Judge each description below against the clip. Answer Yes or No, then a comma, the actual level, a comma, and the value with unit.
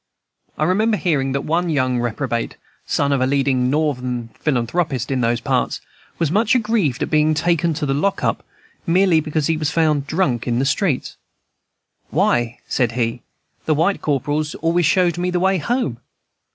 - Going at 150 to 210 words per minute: Yes, average, 170 wpm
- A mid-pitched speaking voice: Yes, medium, 150 Hz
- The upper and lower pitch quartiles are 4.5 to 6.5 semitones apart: Yes, average, 5.1 semitones